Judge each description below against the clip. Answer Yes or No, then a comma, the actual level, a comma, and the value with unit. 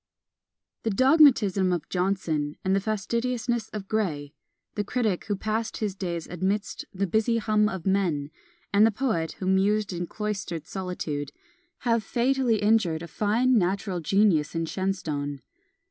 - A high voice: Yes, high, 195 Hz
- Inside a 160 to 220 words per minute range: No, average, 145 wpm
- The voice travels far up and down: No, average, 3.9 semitones